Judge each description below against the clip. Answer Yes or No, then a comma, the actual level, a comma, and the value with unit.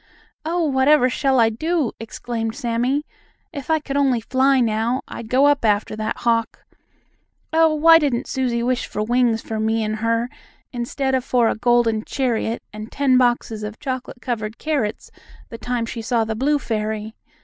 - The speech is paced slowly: No, average, 170 wpm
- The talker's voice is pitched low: No, high, 240 Hz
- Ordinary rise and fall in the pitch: Yes, average, 3.2 semitones